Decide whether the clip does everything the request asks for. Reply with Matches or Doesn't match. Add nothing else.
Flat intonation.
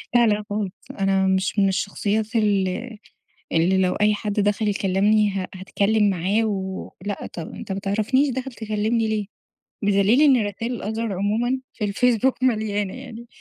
Matches